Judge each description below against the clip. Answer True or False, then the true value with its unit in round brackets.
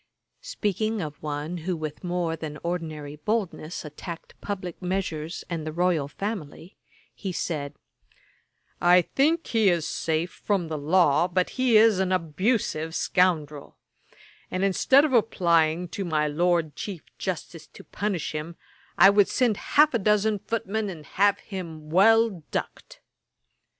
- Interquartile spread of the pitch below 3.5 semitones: False (4.4 semitones)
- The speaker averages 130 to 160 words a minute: True (140 wpm)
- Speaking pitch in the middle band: True (180 Hz)